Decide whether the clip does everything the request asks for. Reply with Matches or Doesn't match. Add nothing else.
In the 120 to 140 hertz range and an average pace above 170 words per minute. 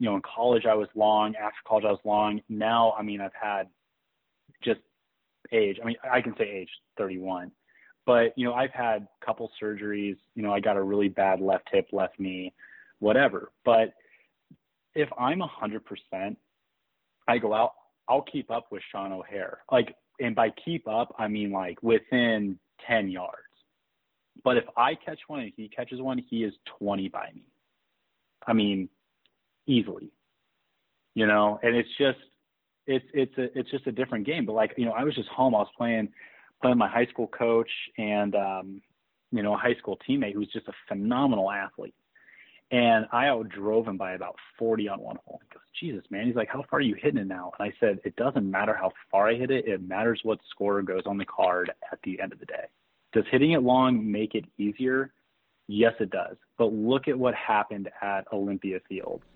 Doesn't match